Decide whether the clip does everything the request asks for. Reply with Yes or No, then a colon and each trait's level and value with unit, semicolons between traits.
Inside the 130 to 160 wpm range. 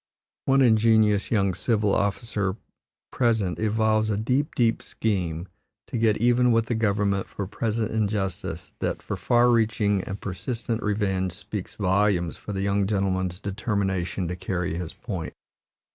Yes: average, 145 wpm